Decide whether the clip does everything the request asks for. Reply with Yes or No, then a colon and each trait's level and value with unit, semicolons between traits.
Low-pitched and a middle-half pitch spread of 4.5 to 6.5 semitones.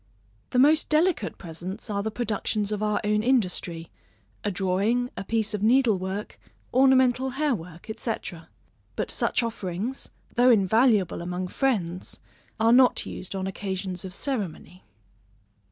No: high, 210 Hz; average, 4.8 semitones